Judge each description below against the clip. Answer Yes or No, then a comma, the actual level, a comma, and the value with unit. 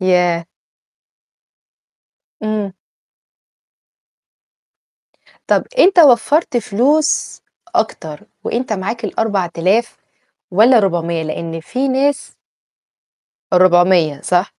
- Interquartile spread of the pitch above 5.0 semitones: Yes, wide, 5.6 semitones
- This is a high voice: Yes, high, 200 Hz